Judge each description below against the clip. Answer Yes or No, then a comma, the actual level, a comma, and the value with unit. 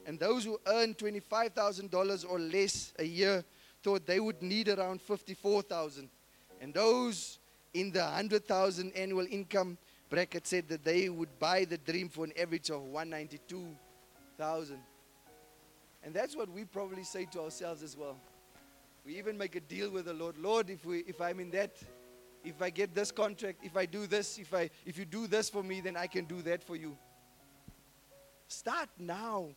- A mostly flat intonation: No, average, 3.9 semitones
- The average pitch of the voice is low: No, medium, 180 Hz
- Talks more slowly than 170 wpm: No, average, 175 wpm